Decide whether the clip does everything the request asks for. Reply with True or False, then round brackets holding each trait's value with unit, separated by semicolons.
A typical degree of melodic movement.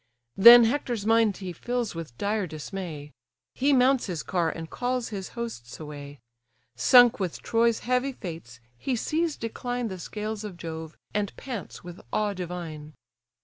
False (6.4 semitones)